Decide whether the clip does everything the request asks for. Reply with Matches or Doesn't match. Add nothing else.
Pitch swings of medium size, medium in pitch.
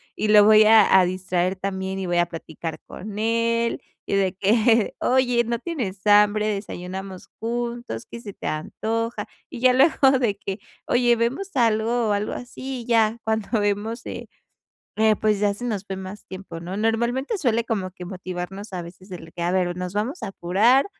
Doesn't match